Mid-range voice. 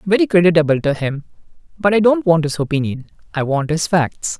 Yes: medium, 170 Hz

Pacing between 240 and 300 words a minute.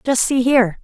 No: fast, 215 wpm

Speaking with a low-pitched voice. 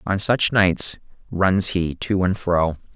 Yes: very low, 95 Hz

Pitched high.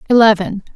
Yes: high, 210 Hz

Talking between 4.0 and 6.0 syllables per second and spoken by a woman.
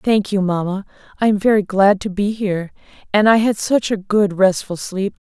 Yes: 5.1 syllables/s; female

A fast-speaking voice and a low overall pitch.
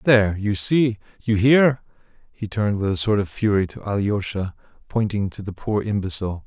No: average, 175 wpm; low, 105 Hz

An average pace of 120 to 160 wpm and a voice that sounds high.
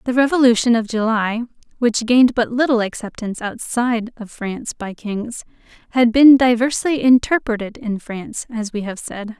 Yes: average, 155 wpm; high, 230 Hz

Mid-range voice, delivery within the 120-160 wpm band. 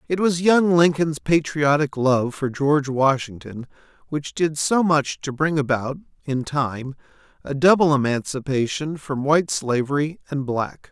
Yes: medium, 145 Hz; average, 145 wpm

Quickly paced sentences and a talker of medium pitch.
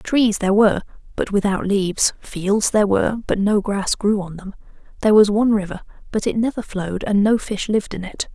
No: fast, 210 wpm; high, 205 Hz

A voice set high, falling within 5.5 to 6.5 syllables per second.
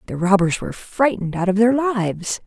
Yes: high, 205 Hz; 5.8 syllables/s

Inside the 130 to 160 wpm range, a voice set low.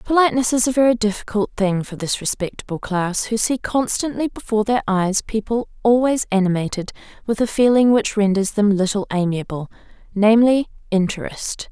No: average, 150 wpm; high, 215 Hz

